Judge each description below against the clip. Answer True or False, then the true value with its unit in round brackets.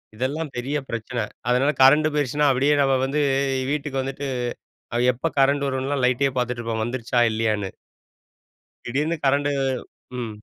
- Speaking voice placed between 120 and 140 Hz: True (135 Hz)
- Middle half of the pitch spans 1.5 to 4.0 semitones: True (2.9 semitones)